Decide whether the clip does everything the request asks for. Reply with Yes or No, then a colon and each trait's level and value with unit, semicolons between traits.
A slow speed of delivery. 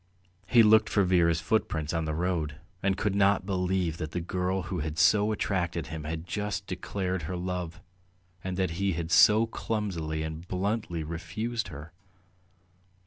No: average, 160 wpm